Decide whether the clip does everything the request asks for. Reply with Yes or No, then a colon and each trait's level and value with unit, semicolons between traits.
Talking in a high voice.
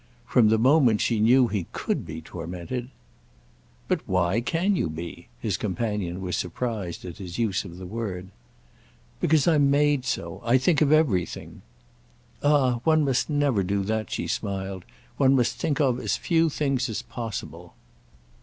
No: low, 115 Hz